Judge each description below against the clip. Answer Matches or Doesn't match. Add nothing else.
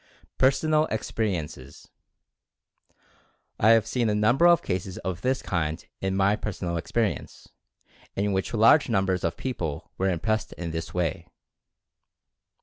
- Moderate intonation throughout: Matches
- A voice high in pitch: Doesn't match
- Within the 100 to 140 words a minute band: Matches